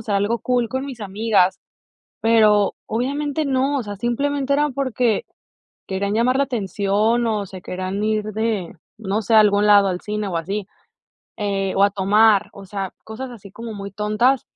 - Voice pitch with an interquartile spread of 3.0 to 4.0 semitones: Yes, average, 3.3 semitones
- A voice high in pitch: Yes, high, 215 Hz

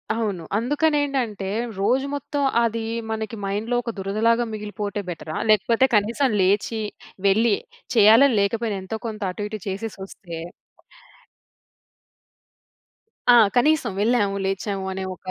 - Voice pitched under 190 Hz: No, high, 215 Hz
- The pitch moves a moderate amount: Yes, average, 3.0 semitones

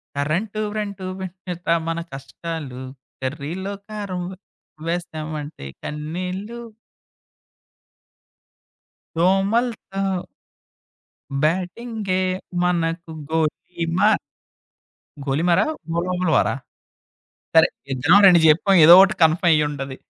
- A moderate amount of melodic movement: Yes, average, 3.6 semitones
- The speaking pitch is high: No, medium, 175 Hz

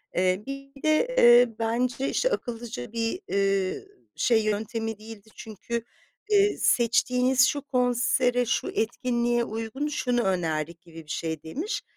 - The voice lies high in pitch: Yes, high, 235 Hz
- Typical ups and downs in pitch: Yes, average, 3.5 semitones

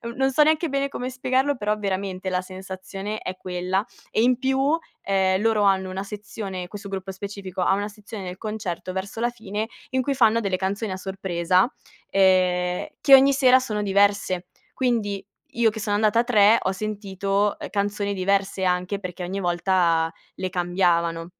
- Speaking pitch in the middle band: No, high, 200 Hz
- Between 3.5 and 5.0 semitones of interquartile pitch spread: No, average, 2.8 semitones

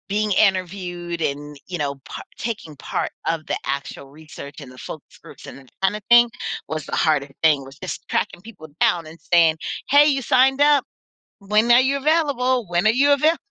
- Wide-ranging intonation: Yes, wide, 8.2 semitones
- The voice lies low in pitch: No, medium, 185 Hz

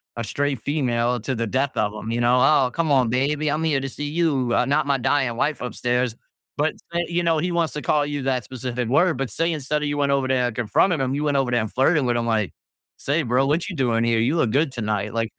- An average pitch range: Yes, average, 3.8 semitones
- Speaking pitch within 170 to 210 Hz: No, low, 135 Hz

